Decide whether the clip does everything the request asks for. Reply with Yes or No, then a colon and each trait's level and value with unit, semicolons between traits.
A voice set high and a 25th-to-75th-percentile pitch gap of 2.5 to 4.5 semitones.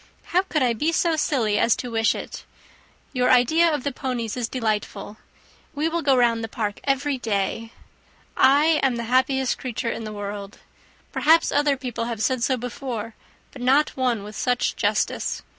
Yes: very high, 250 Hz; average, 3.6 semitones